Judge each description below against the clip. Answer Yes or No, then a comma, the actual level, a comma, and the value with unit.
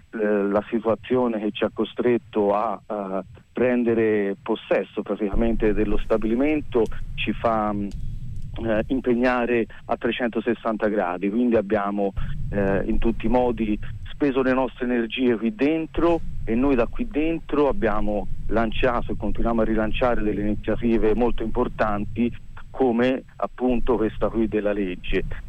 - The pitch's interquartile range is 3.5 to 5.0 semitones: No, narrow, 2.6 semitones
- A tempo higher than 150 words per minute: No, average, 120 wpm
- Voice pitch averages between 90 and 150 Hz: Yes, low, 115 Hz